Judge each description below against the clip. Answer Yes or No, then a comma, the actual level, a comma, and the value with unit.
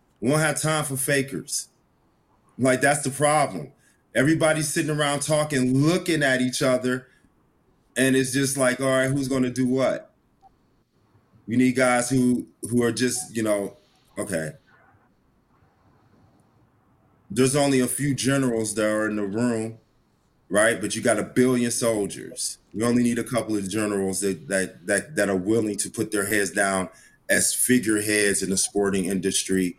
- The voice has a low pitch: Yes, low, 125 Hz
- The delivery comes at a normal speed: Yes, average, 160 wpm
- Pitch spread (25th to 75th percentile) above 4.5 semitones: No, average, 4.0 semitones